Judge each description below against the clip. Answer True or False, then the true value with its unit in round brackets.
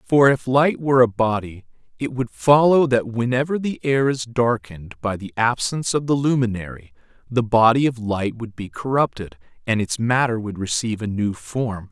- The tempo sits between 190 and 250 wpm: False (180 wpm)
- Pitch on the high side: False (120 Hz)